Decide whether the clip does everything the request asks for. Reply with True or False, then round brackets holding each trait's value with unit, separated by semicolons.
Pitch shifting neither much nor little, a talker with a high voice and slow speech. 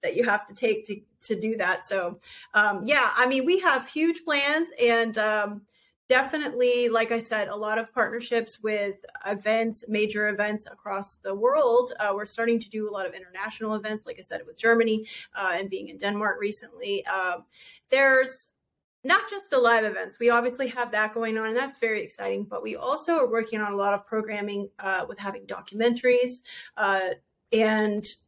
False (3.2 semitones; 225 Hz; 190 wpm)